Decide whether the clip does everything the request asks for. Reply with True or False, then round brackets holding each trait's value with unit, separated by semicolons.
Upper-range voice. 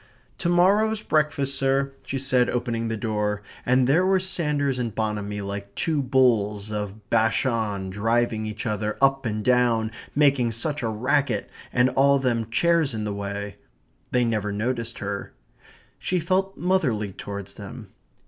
False (120 Hz)